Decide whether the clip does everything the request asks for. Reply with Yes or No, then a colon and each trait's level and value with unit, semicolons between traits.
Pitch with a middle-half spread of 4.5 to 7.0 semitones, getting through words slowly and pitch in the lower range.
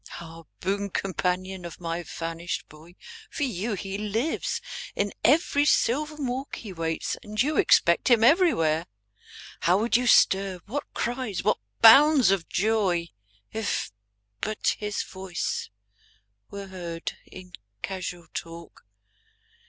No: wide, 5.4 semitones; slow, 125 wpm; high, 195 Hz